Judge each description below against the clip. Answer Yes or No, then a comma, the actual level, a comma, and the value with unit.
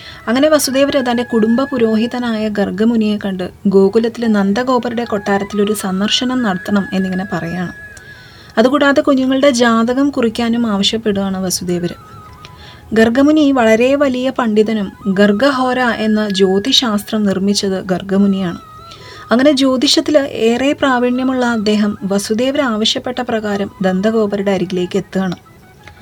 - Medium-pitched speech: No, high, 220 Hz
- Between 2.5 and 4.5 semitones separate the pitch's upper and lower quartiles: Yes, average, 4.2 semitones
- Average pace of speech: Yes, average, 90 wpm